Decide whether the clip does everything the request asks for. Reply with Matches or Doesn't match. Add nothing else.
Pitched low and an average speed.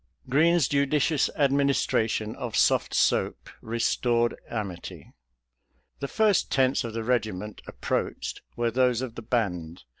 Doesn't match